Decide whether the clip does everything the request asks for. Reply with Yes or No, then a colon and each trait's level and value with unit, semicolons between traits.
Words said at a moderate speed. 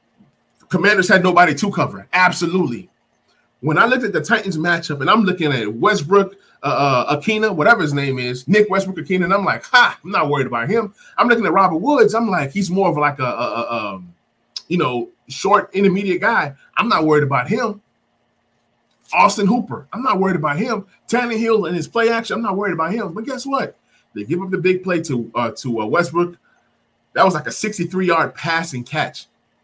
No: fast, 210 wpm